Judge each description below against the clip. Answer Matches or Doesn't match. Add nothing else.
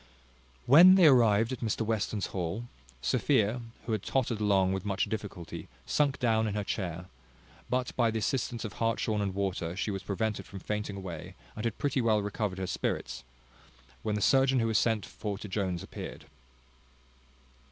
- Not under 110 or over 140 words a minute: Doesn't match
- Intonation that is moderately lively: Matches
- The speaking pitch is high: Doesn't match